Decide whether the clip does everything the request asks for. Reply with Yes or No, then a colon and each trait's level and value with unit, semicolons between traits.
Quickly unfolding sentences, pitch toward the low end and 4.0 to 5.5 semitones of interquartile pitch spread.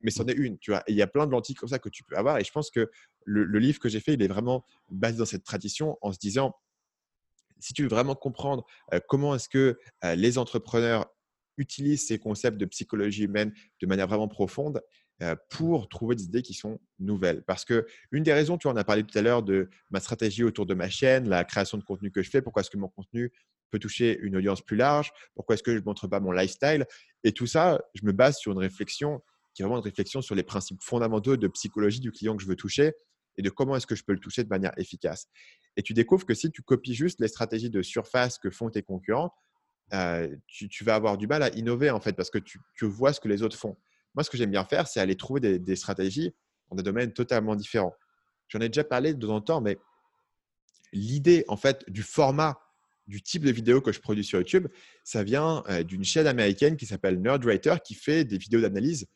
Yes: fast, 245 wpm; low, 110 Hz; average, 4.8 semitones